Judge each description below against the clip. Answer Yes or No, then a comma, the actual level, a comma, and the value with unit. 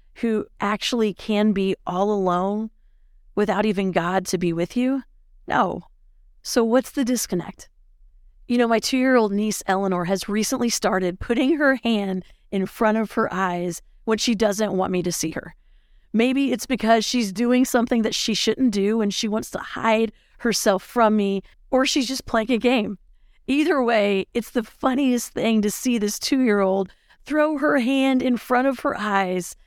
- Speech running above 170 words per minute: Yes, average, 180 wpm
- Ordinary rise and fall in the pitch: Yes, average, 4.1 semitones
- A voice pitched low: No, high, 220 Hz